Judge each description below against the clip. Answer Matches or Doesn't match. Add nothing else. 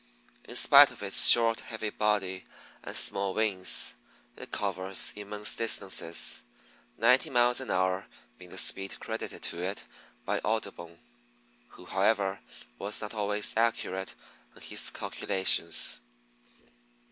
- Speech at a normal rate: Doesn't match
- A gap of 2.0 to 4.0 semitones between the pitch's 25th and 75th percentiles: Matches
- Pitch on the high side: Doesn't match